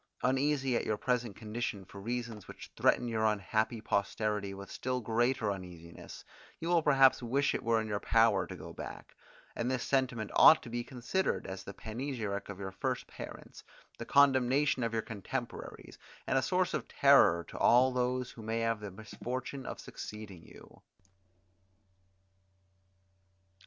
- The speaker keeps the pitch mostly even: No, average, 3.4 semitones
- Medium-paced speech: Yes, average, 160 wpm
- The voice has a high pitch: No, low, 115 Hz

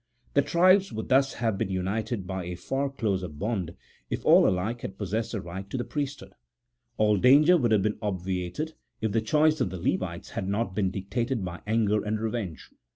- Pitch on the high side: No, low, 105 Hz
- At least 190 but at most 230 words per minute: Yes, average, 195 wpm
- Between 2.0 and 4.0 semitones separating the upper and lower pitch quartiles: No, average, 4.4 semitones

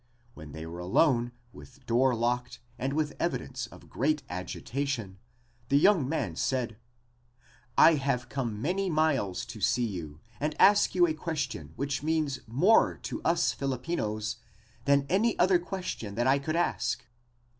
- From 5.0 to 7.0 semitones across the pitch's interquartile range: Yes, wide, 5.5 semitones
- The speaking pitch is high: No, low, 135 Hz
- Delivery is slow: No, average, 150 wpm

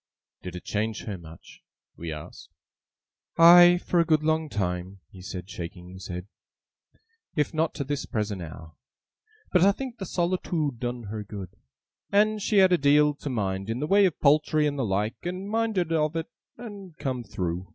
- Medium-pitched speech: Yes, medium, 145 Hz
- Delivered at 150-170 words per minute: No, average, 185 wpm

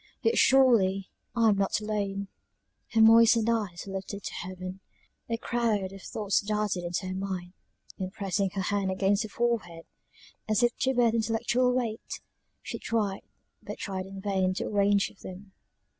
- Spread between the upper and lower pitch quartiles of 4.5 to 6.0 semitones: No, average, 2.9 semitones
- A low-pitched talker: No, high, 200 Hz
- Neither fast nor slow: Yes, average, 170 wpm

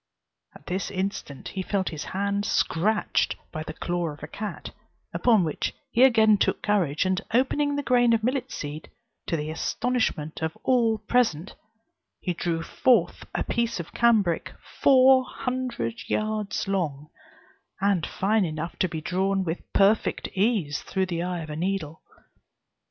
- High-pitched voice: Yes, high, 195 Hz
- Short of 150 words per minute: No, average, 155 wpm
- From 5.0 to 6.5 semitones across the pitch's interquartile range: Yes, wide, 5.5 semitones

